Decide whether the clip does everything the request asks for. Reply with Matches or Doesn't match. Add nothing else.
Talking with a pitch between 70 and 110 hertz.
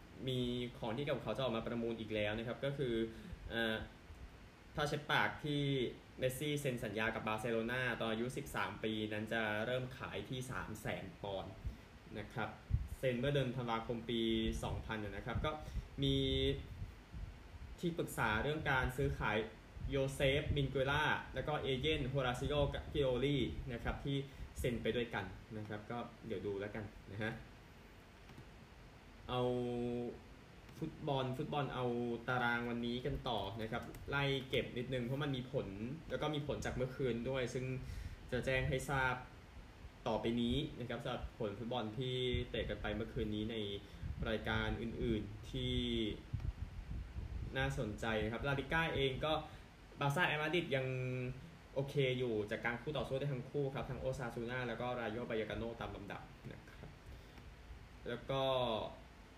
Doesn't match